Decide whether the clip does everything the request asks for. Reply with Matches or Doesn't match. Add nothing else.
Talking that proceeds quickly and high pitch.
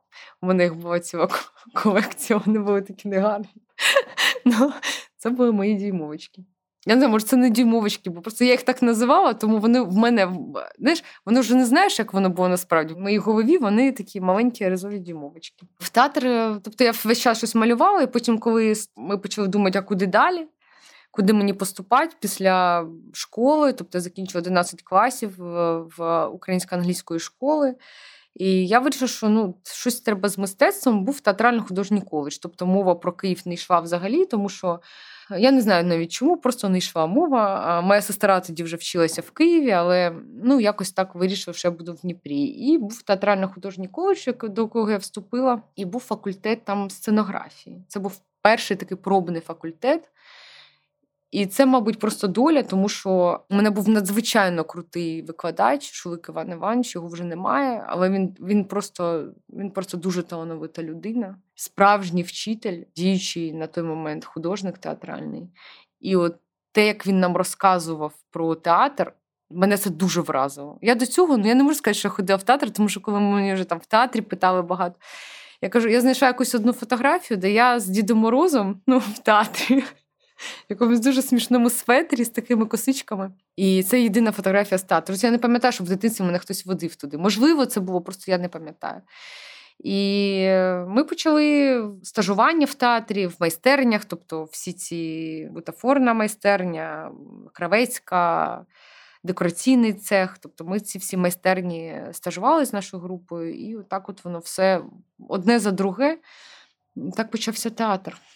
Matches